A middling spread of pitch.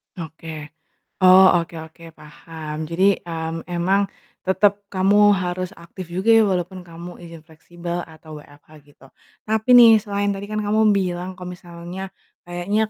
Yes: average, 3.0 semitones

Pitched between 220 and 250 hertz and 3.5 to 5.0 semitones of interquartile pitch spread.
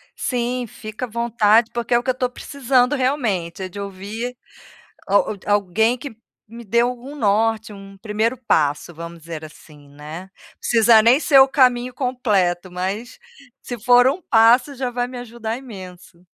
Yes: high, 225 Hz; average, 4.2 semitones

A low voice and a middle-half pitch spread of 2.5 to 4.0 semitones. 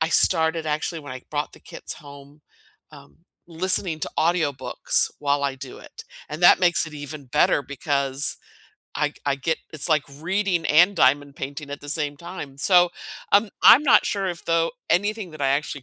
No: medium, 155 Hz; average, 3.4 semitones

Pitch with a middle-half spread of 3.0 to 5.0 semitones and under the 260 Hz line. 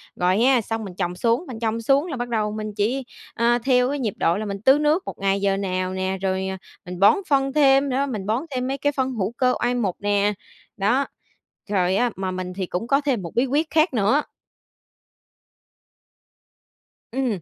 No: wide, 5.5 semitones; high, 225 Hz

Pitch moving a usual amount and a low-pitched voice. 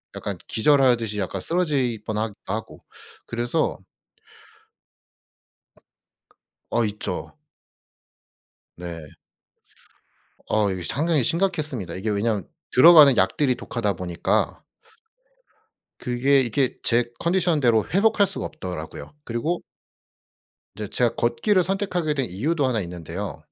No: wide, 6.9 semitones; low, 120 Hz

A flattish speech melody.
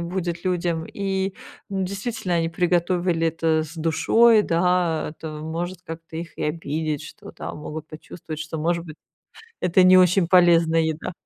Yes: narrow, 2.1 semitones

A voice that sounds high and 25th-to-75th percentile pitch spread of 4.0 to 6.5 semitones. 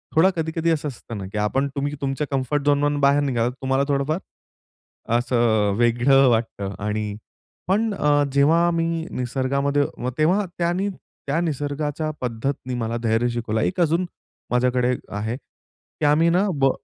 No: medium, 140 Hz; average, 4.4 semitones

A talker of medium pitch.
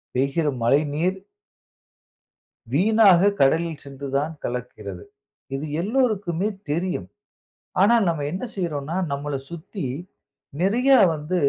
Yes: medium, 165 Hz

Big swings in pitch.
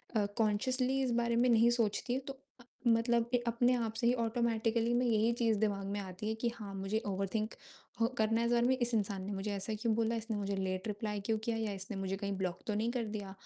No: narrow, 2.6 semitones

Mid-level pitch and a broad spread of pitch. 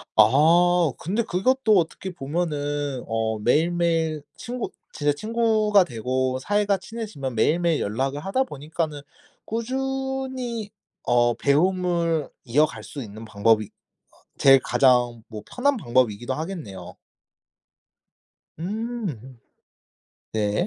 Yes: medium, 155 Hz; wide, 8.2 semitones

